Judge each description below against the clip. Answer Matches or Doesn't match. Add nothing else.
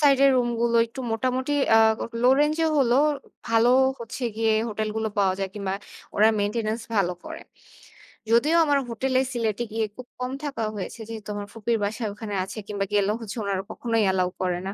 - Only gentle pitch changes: Doesn't match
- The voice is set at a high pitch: Matches